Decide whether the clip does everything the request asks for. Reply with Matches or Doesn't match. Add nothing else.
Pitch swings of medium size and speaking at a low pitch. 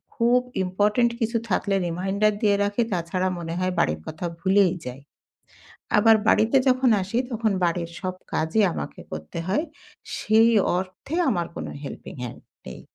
Doesn't match